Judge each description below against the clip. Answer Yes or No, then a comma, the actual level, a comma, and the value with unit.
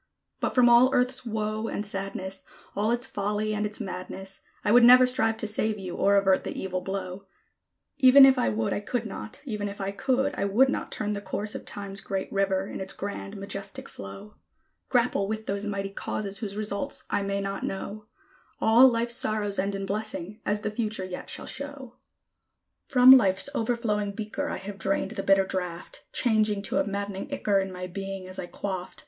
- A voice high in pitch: Yes, high, 205 Hz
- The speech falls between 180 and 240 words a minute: Yes, average, 195 wpm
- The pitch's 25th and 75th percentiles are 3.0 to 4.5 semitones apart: No, narrow, 2.4 semitones